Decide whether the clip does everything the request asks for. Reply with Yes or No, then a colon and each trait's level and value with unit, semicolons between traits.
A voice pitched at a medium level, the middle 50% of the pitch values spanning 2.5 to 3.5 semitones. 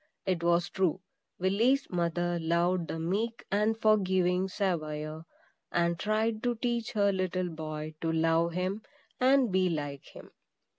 No: medium, 180 Hz; average, 4.0 semitones